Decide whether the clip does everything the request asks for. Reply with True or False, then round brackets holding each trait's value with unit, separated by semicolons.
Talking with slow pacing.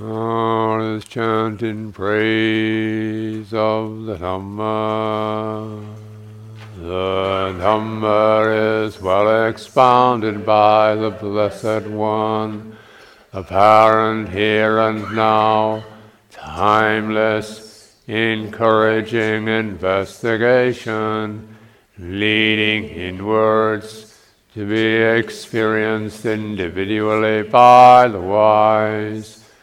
True (65 wpm)